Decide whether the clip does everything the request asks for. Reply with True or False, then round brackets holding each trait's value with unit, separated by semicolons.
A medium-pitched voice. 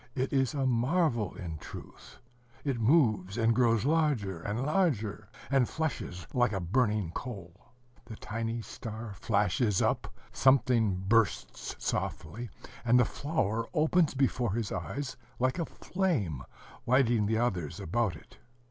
False (115 Hz)